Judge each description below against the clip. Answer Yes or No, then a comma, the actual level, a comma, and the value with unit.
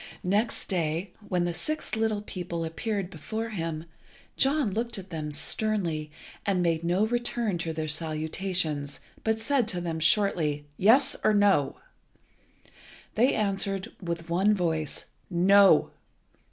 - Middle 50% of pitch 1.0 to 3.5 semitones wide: No, average, 4.7 semitones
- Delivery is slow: Yes, slow, 130 wpm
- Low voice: No, medium, 185 Hz